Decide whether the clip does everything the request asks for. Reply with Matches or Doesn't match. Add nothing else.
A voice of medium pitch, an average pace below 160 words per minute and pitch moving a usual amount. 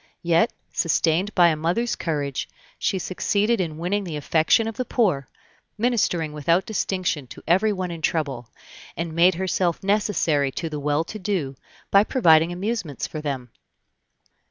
Matches